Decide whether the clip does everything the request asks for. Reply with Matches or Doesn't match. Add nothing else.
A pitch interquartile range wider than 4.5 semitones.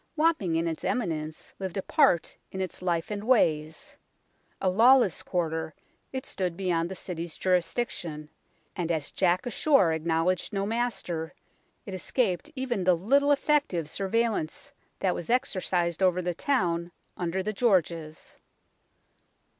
Matches